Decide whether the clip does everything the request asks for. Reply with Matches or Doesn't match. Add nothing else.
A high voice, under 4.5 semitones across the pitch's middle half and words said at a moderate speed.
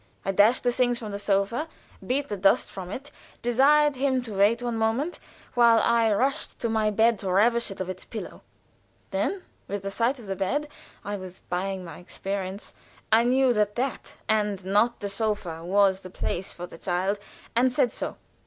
Matches